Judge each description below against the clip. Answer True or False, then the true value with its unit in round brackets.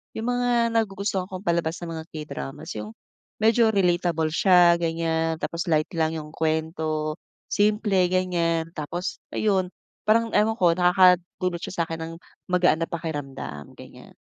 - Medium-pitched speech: True (170 Hz)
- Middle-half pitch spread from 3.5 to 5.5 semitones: False (2.9 semitones)